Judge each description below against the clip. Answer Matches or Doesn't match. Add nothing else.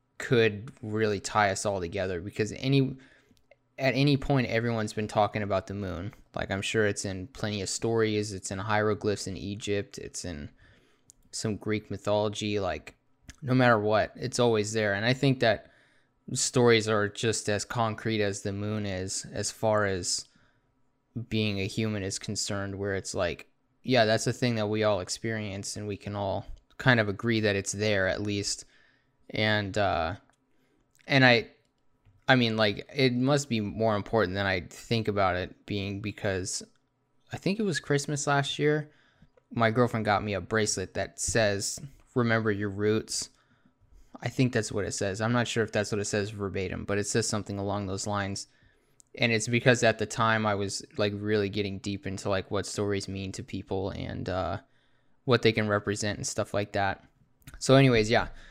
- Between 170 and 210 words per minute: Matches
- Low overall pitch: Matches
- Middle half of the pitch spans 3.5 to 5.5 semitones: Doesn't match